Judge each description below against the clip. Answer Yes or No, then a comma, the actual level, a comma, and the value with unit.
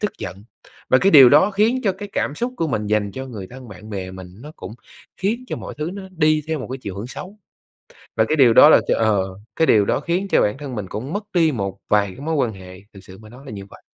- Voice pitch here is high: No, low, 130 Hz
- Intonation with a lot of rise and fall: Yes, wide, 7.9 semitones